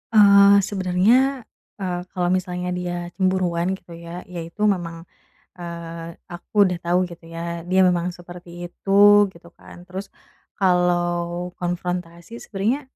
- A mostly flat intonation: Yes, narrow, 1.7 semitones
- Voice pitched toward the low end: No, medium, 180 Hz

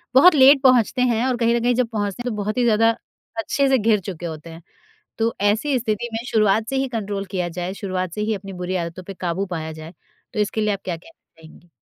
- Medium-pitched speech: No, high, 215 Hz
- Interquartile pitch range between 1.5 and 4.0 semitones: No, average, 4.5 semitones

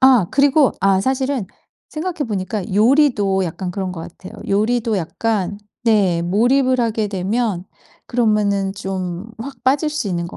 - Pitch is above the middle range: Yes, high, 210 Hz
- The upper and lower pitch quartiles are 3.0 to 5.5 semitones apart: Yes, average, 5.1 semitones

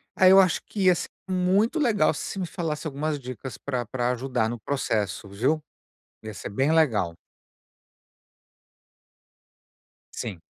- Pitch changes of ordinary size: No, wide, 7.7 semitones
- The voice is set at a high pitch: No, medium, 140 Hz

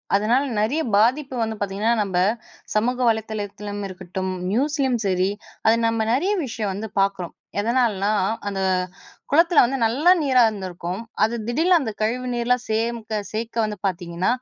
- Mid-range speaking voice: No, high, 220 Hz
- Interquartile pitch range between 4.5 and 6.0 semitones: No, average, 3.8 semitones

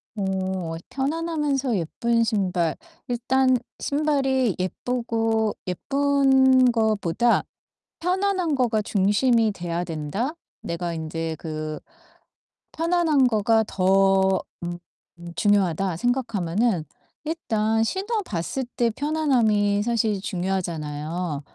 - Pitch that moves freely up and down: Yes, wide, 6.3 semitones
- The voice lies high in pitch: Yes, high, 220 Hz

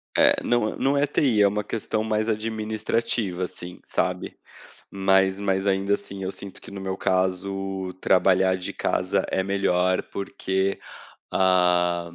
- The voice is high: No, very low, 95 Hz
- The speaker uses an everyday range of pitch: No, narrow, 2.2 semitones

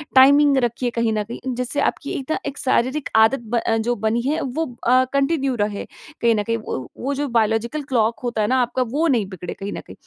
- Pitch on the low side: No, high, 245 Hz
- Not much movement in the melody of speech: No, average, 3.6 semitones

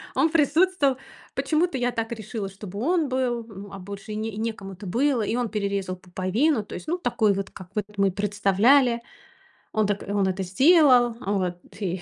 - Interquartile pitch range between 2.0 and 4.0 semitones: No, average, 4.7 semitones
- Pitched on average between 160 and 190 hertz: No, high, 215 Hz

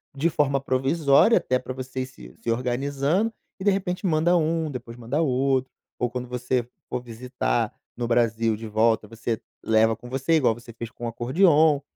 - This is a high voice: No, low, 130 Hz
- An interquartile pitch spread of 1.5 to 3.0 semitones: No, average, 4.0 semitones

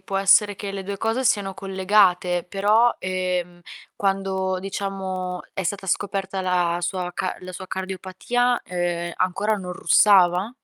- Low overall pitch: No, high, 190 Hz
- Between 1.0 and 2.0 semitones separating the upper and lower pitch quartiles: Yes, narrow, 1.5 semitones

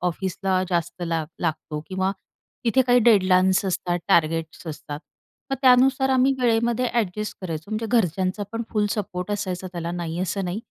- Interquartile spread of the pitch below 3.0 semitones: No, average, 4.3 semitones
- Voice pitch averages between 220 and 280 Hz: No, medium, 185 Hz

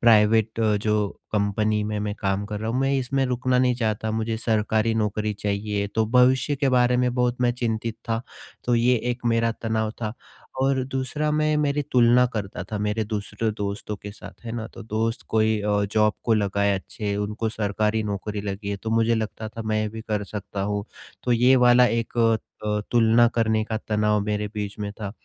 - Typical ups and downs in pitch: No, narrow, 2.2 semitones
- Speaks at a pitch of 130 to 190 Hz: No, low, 110 Hz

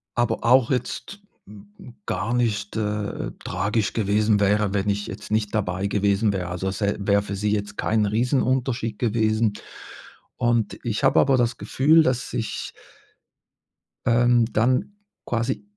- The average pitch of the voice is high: No, low, 110 Hz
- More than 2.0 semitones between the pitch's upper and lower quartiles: Yes, average, 2.7 semitones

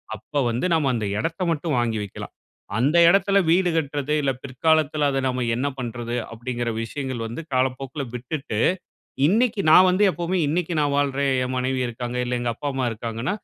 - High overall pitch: No, low, 135 Hz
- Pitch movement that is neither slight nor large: Yes, average, 4.4 semitones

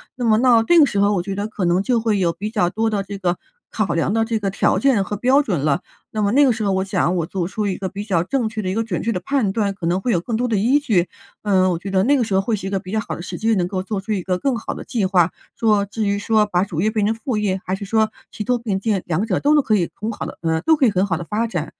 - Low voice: No, high, 205 Hz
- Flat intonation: No, average, 3.2 semitones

